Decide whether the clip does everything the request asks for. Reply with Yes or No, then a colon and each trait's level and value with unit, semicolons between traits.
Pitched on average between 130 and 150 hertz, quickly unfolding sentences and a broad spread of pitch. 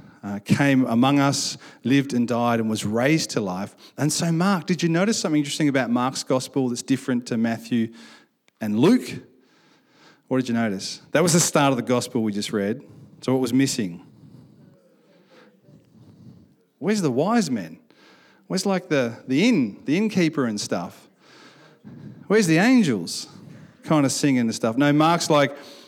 No: medium, 140 Hz; average, 165 wpm; wide, 5.9 semitones